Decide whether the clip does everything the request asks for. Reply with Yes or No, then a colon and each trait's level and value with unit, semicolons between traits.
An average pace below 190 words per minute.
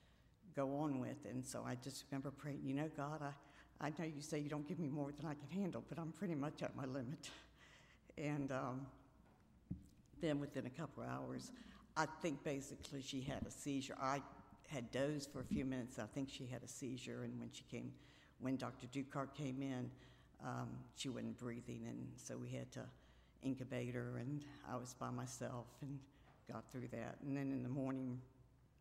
No: average, 200 wpm